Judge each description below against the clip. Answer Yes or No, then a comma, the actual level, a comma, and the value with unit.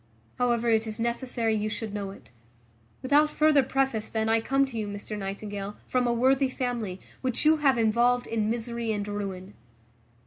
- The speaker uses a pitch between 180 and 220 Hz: No, high, 230 Hz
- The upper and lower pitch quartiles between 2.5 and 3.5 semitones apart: Yes, average, 3.2 semitones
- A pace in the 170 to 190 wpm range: Yes, average, 175 wpm